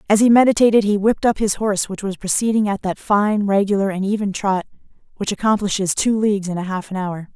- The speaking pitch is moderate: No, high, 200 Hz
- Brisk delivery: Yes, fast, 220 wpm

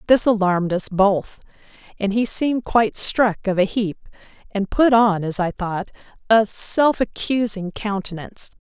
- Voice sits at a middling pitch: No, high, 205 Hz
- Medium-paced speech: Yes, average, 155 wpm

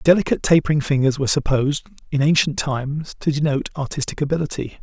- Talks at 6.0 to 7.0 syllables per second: Yes, 6.9 syllables/s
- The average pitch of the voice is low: No, medium, 145 Hz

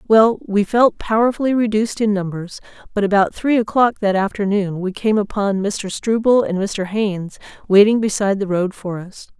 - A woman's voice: Yes, female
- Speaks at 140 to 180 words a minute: Yes, average, 170 wpm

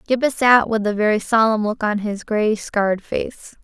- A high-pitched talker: Yes, high, 215 Hz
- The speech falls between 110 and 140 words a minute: No, average, 200 wpm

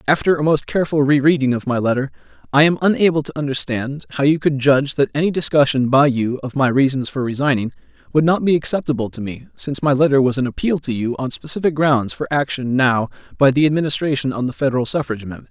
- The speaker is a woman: No, male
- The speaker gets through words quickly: Yes, fast, 215 wpm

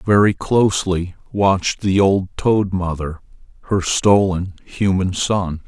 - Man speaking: Yes, male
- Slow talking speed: Yes, slow, 115 wpm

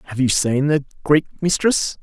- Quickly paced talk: No, average, 180 wpm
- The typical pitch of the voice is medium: Yes, medium, 145 Hz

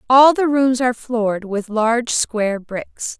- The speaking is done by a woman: Yes, female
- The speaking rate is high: No, average, 170 wpm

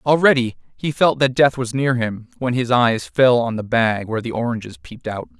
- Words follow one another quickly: Yes, fast, 225 wpm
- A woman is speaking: No, male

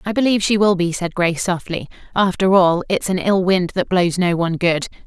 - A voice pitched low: No, medium, 180 Hz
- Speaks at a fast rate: Yes, fast, 225 wpm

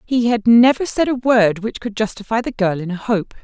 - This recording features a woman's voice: Yes, female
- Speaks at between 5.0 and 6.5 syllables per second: Yes, 5.2 syllables/s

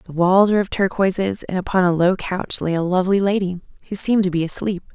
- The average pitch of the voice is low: No, medium, 185 Hz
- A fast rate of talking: Yes, fast, 230 wpm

